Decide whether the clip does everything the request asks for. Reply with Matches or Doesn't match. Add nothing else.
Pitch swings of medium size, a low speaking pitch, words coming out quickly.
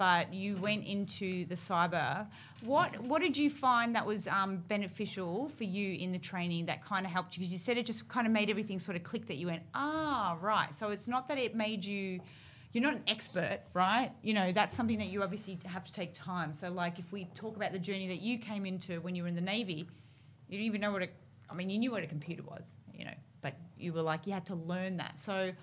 Doesn't match